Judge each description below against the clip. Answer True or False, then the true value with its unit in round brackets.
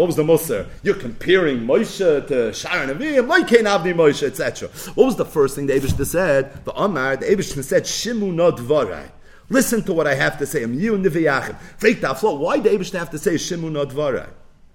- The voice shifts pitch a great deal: True (6.0 semitones)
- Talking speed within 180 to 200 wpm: True (195 wpm)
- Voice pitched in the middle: True (175 Hz)